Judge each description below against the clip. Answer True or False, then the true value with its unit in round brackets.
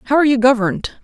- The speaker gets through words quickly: True (230 wpm)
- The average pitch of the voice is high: True (250 Hz)